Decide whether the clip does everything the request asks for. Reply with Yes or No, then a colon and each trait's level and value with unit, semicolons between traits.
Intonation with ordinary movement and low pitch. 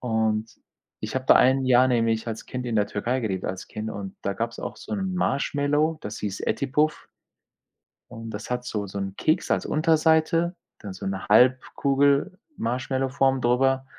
Yes: average, 4.2 semitones; low, 125 Hz